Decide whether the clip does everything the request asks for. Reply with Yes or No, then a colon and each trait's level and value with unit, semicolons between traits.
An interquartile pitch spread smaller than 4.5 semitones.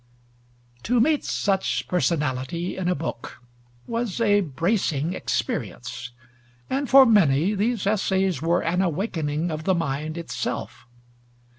No: wide, 5.5 semitones